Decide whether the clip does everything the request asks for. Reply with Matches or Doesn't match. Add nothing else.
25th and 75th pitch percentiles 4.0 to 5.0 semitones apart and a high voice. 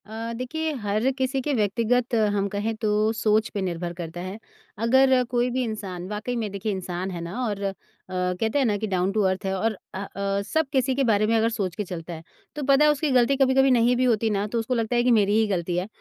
Matches